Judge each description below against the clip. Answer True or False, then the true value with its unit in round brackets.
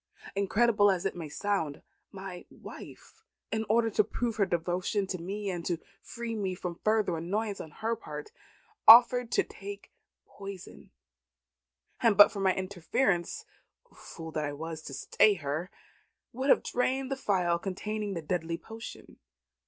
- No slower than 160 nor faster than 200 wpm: False (150 wpm)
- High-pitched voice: True (195 Hz)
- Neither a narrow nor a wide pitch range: True (4.2 semitones)